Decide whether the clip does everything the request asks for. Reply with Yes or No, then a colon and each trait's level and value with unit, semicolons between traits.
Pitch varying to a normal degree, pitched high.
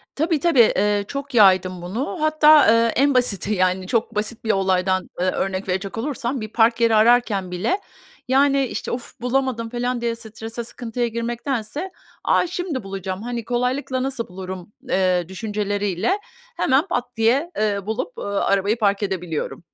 Yes: average, 4.5 semitones; high, 225 Hz